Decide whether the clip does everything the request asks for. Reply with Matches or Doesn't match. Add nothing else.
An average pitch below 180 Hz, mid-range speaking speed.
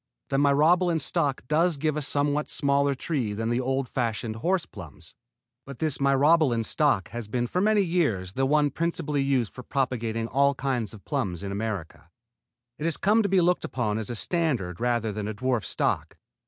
Matches